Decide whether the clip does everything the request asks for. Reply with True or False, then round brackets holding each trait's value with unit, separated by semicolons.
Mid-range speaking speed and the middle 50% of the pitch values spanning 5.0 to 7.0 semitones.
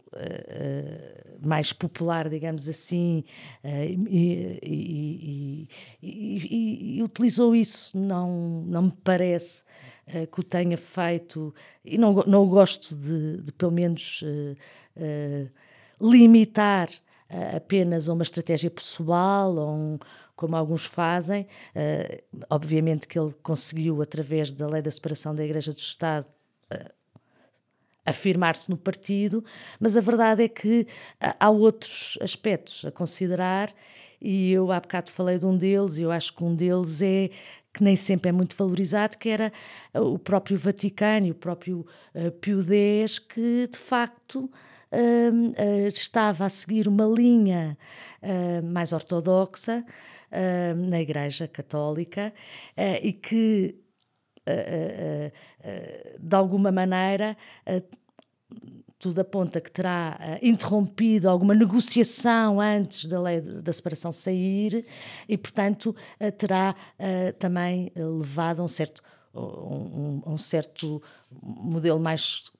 False (135 wpm; 3.9 semitones)